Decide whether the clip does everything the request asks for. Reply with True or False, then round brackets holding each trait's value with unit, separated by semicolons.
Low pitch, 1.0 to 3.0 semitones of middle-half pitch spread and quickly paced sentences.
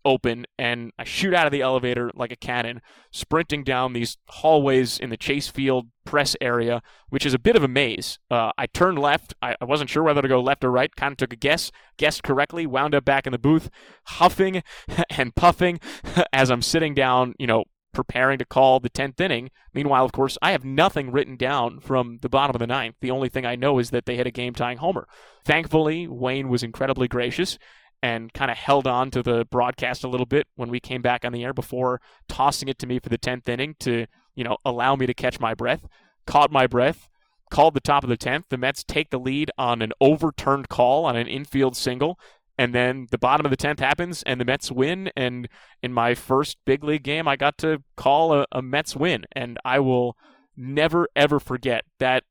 True (130 Hz; 2.7 semitones; 220 wpm)